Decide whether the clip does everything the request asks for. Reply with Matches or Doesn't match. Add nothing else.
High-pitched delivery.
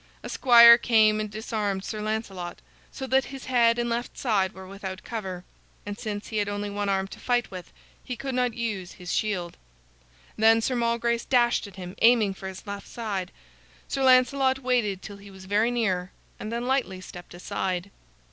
Matches